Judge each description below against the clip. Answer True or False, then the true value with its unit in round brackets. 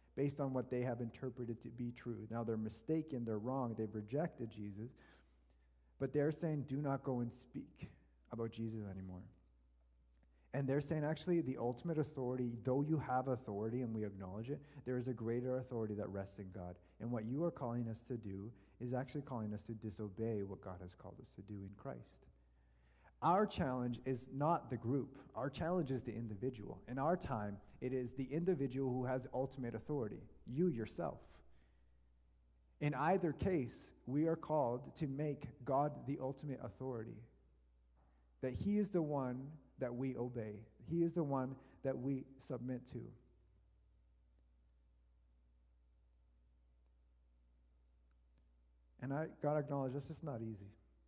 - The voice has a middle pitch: False (120 Hz)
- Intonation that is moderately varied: False (7.1 semitones)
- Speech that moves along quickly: False (160 wpm)